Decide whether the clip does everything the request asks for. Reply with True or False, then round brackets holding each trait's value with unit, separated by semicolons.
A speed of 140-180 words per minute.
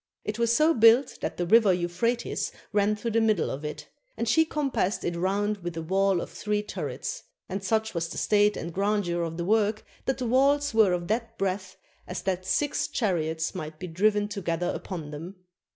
False (200 wpm)